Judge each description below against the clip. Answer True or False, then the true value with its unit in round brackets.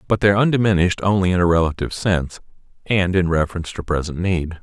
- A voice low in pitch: True (90 Hz)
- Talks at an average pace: True (195 wpm)